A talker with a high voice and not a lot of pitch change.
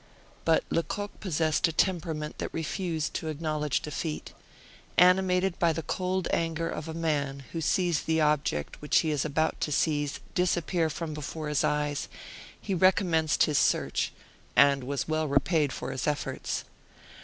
No: medium, 160 Hz; narrow, 2.3 semitones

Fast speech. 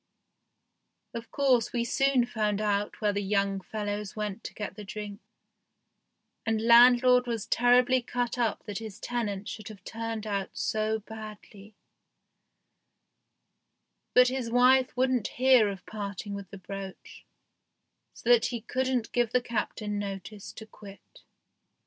No: slow, 135 wpm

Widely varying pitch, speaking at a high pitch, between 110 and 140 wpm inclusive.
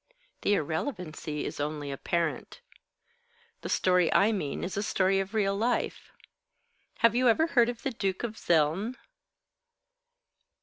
Yes: wide, 6.1 semitones; high, 195 Hz; slow, 135 wpm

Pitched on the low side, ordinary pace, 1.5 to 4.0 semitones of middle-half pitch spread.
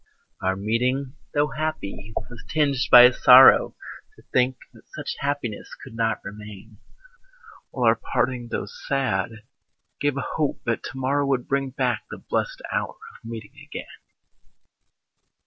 Yes: low, 125 Hz; average, 145 wpm; average, 3.5 semitones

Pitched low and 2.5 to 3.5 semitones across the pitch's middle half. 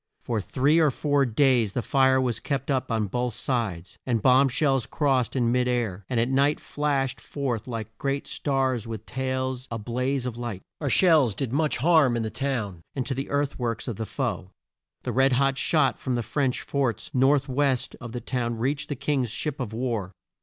Yes: low, 130 Hz; average, 2.8 semitones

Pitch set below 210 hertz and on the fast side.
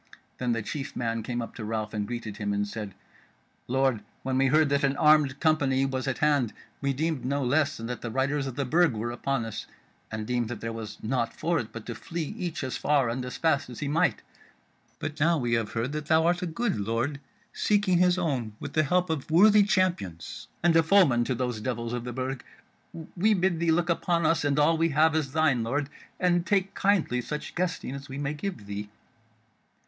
Yes: medium, 140 Hz; fast, 220 wpm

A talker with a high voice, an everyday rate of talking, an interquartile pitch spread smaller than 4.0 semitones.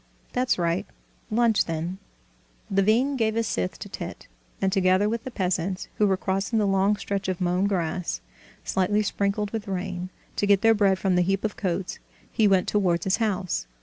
Yes: high, 195 Hz; average, 180 wpm; narrow, 2.4 semitones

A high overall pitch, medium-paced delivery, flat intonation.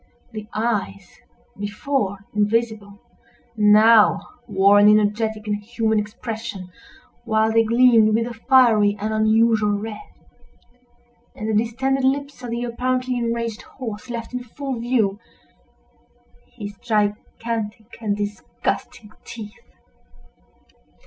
No: high, 220 Hz; slow, 110 wpm; narrow, 2.1 semitones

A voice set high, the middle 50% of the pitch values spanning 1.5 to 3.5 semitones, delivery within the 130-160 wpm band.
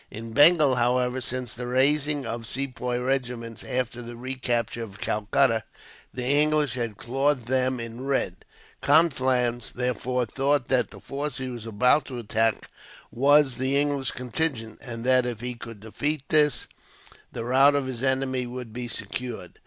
No: low, 125 Hz; narrow, 2.5 semitones; average, 155 wpm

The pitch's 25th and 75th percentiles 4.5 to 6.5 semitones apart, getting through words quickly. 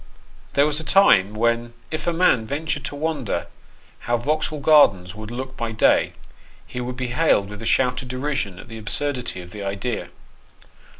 No: average, 5.3 semitones; average, 175 wpm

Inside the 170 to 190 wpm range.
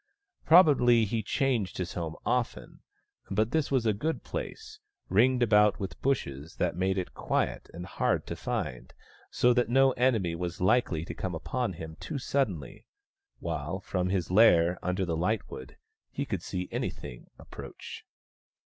No: average, 155 wpm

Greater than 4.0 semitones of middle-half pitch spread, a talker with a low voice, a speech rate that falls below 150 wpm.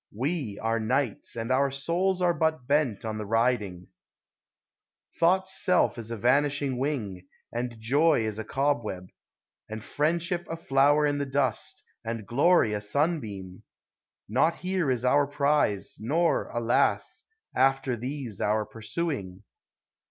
Yes: average, 5.2 semitones; low, 130 Hz; slow, 135 wpm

